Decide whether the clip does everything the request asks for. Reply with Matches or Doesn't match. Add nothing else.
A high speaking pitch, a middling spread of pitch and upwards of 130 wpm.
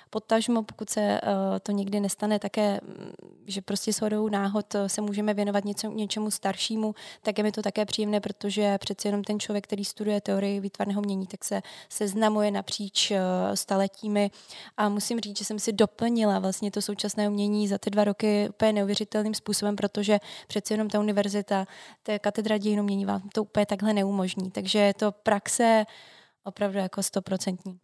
Doesn't match